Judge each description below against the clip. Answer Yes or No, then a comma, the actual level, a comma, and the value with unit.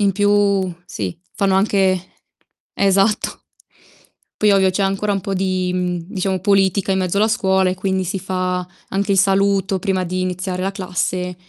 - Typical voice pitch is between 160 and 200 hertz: Yes, high, 190 Hz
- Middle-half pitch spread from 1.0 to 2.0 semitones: Yes, narrow, 1.3 semitones